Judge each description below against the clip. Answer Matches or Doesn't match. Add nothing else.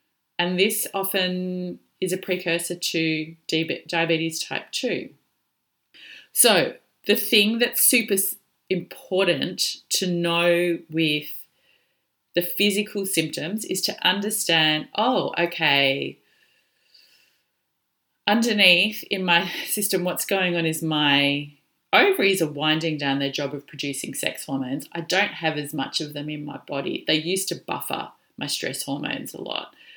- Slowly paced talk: Matches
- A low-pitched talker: Doesn't match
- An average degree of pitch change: Matches